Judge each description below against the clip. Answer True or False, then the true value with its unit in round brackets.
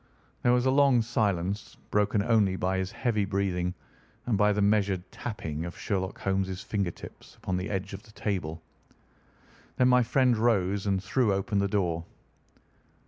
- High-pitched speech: False (100 Hz)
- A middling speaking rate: True (165 wpm)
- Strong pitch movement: False (2.8 semitones)